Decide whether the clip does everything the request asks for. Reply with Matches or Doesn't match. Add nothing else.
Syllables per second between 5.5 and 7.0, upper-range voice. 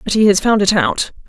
Matches